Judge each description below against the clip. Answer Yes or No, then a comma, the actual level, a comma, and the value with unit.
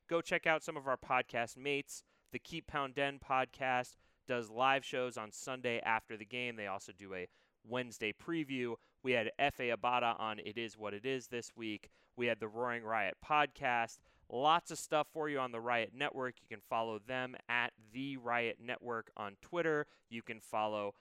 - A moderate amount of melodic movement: Yes, average, 3.2 semitones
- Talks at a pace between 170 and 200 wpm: Yes, average, 190 wpm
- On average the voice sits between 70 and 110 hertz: No, low, 120 Hz